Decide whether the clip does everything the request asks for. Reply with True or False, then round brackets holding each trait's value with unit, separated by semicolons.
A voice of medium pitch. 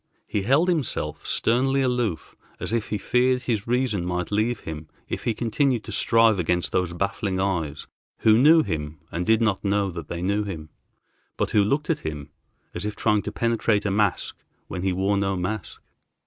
False (105 Hz)